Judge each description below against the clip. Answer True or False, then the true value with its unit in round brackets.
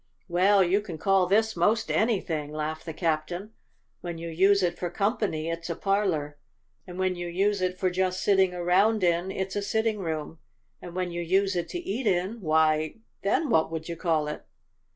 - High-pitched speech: False (180 Hz)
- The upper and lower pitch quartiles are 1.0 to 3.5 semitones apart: True (3.1 semitones)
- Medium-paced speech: True (195 wpm)